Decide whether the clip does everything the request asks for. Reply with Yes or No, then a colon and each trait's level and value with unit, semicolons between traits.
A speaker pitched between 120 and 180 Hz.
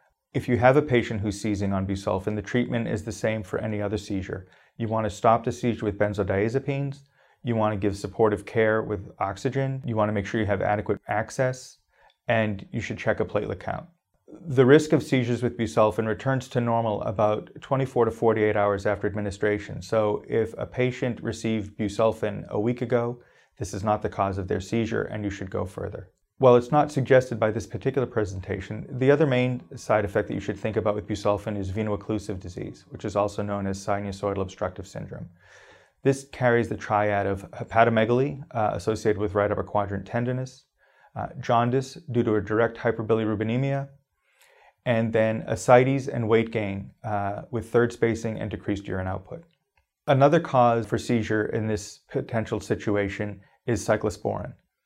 No: low, 110 Hz